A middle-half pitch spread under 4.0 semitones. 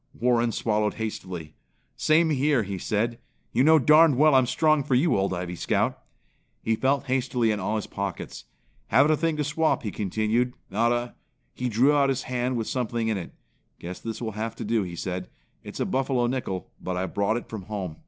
No: average, 4.4 semitones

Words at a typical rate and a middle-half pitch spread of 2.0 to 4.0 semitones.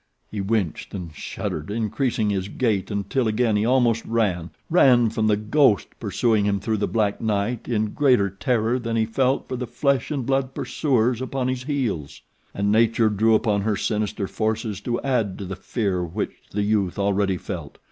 Yes: average, 180 wpm; average, 3.4 semitones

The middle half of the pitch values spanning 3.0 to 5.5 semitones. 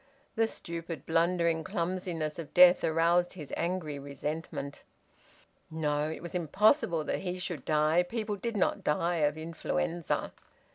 No: narrow, 2.6 semitones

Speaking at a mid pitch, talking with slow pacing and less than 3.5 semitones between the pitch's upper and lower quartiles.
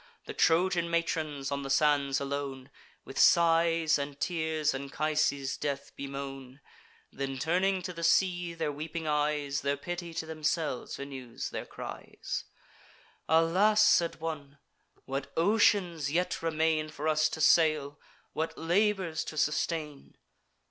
Yes: medium, 155 Hz; slow, 130 wpm; average, 2.9 semitones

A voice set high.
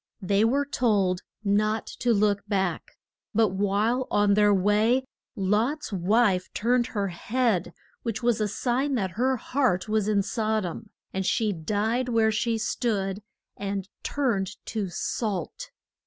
Yes: high, 215 Hz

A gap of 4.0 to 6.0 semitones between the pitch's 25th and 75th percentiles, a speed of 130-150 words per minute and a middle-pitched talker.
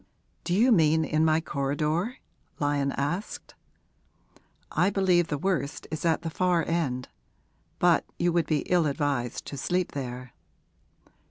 No: average, 3.6 semitones; average, 140 wpm; medium, 160 Hz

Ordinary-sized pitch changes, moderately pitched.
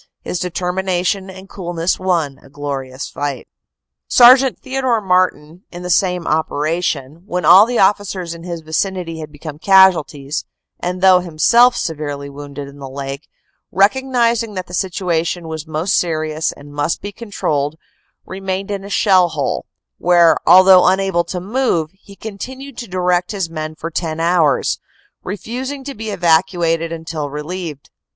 Yes: average, 3.6 semitones; medium, 175 Hz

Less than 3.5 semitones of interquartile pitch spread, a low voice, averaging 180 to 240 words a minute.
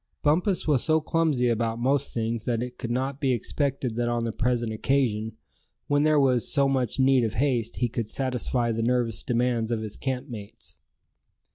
Yes: average, 2.9 semitones; low, 125 Hz; average, 185 wpm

